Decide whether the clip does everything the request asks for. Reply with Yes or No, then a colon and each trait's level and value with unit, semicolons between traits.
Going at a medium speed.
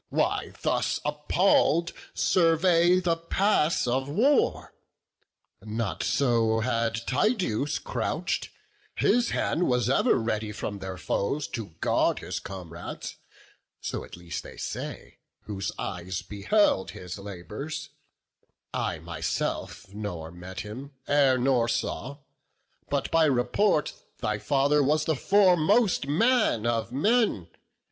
No: slow, 115 wpm